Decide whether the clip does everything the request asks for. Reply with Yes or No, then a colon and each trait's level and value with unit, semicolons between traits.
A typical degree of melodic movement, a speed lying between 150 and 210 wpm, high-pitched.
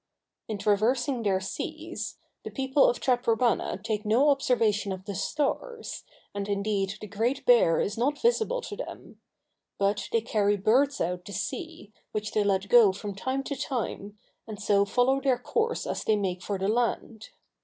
Yes: average, 4.6 semitones; average, 170 wpm; high, 220 Hz